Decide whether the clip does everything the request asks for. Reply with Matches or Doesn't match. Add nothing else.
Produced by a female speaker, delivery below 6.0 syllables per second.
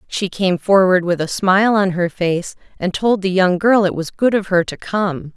Matches